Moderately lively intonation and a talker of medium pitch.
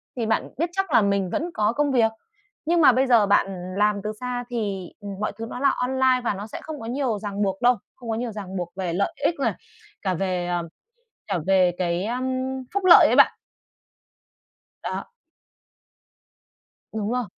No: average, 4.8 semitones; high, 225 Hz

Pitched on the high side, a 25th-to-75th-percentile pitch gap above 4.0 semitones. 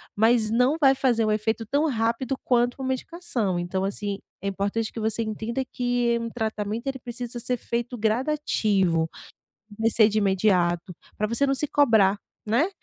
No: high, 225 Hz; average, 3.0 semitones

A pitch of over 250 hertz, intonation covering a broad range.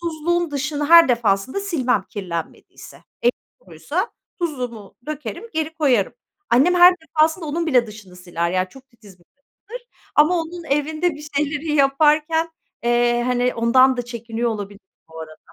Yes: very high, 275 Hz; wide, 5.8 semitones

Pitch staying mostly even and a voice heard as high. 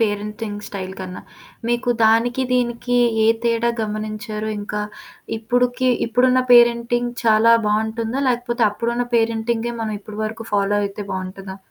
Yes: narrow, 2.2 semitones; high, 225 Hz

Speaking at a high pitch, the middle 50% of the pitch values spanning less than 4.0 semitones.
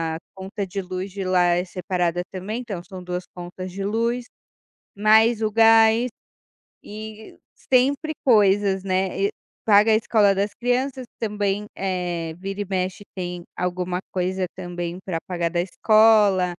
Yes: high, 195 Hz; average, 3.2 semitones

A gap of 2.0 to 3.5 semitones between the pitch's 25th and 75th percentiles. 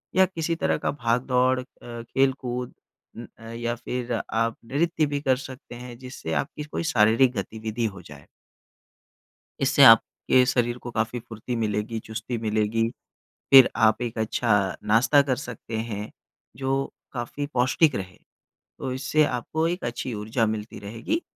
Yes: average, 2.9 semitones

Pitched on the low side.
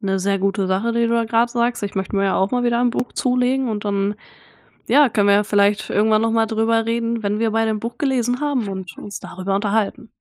No: high, 220 Hz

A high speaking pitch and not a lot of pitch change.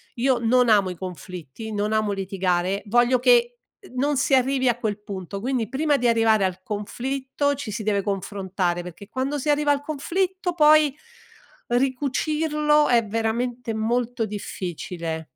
No: high, 235 Hz; average, 5.3 semitones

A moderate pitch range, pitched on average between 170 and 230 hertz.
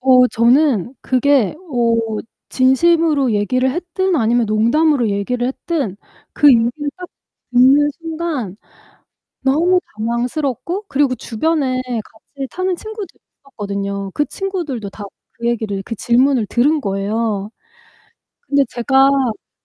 No: average, 4.7 semitones; very high, 255 Hz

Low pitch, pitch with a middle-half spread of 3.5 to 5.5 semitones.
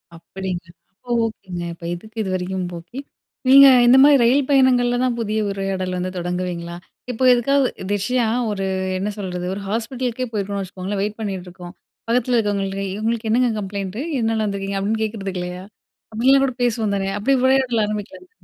No: high, 205 Hz; average, 4.2 semitones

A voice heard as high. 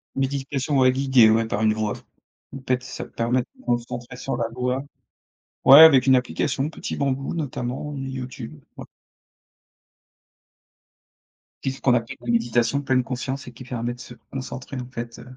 No: low, 130 Hz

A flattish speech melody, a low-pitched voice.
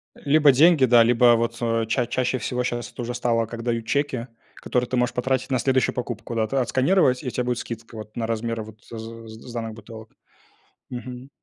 Yes: narrow, 1.8 semitones; low, 120 Hz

